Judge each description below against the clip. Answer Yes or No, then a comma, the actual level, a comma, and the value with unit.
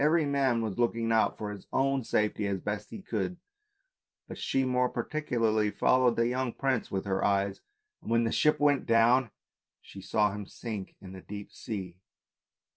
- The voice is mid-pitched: No, low, 115 Hz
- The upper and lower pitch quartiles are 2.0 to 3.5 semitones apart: No, average, 3.9 semitones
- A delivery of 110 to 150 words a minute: No, average, 180 wpm